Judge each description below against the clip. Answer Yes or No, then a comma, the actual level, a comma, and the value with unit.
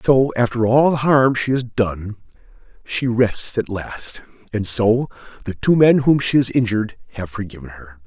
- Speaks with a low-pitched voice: Yes, low, 115 Hz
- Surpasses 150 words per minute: Yes, average, 180 wpm